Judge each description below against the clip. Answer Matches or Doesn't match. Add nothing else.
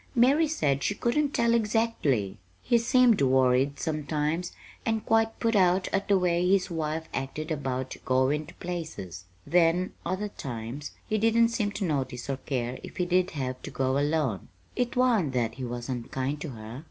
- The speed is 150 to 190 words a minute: Matches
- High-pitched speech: Doesn't match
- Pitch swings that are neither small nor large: Doesn't match